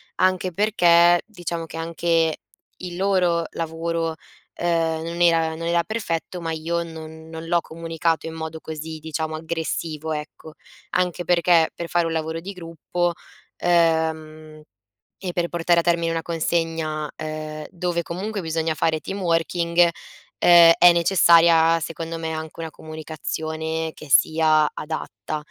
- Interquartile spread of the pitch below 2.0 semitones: Yes, narrow, 1.3 semitones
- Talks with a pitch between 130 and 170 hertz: Yes, medium, 165 Hz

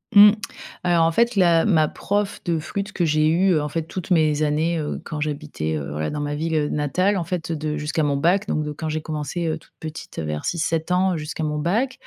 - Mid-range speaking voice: Yes, medium, 160 Hz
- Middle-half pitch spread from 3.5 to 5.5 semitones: No, average, 2.8 semitones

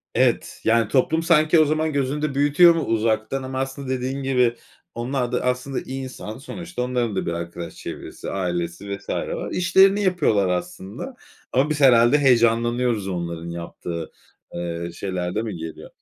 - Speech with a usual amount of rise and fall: No, wide, 6.4 semitones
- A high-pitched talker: No, low, 125 Hz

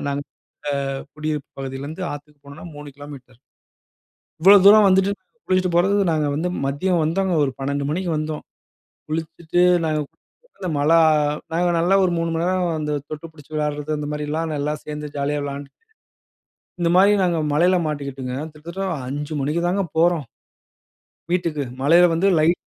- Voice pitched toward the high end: No, medium, 155 Hz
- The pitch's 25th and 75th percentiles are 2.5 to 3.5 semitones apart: Yes, average, 3.2 semitones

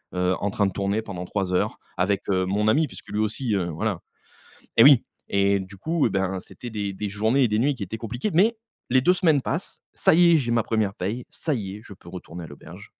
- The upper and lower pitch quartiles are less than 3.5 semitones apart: No, average, 4.5 semitones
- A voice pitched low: Yes, low, 105 Hz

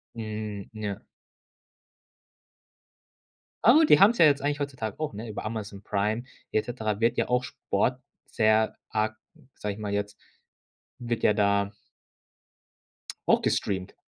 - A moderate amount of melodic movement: Yes, average, 3.1 semitones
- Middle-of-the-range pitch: No, low, 110 Hz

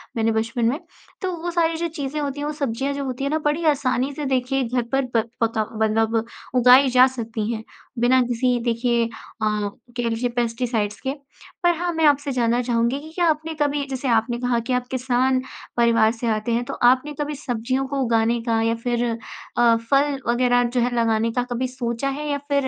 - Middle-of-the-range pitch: No, very high, 250 Hz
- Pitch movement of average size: Yes, average, 3.1 semitones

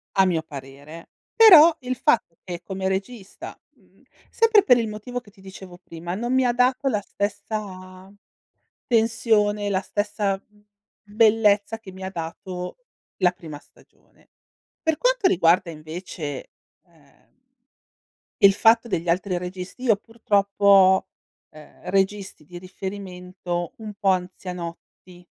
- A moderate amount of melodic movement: Yes, average, 3.4 semitones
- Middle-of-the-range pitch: No, high, 195 Hz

